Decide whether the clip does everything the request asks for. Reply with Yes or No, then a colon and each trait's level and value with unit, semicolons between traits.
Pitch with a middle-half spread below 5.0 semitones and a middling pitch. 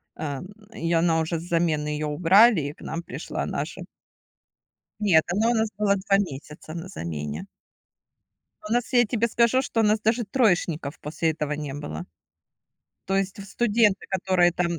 No: wide, 5.5 semitones; medium, 175 Hz